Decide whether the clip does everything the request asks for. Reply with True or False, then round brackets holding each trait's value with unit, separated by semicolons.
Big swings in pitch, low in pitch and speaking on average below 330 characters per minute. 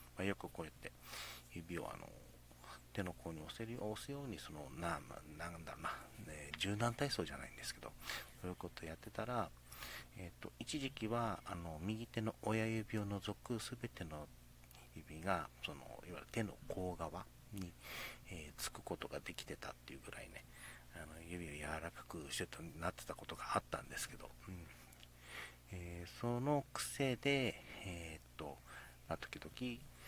True (7.2 semitones; 90 Hz; 290 characters per minute)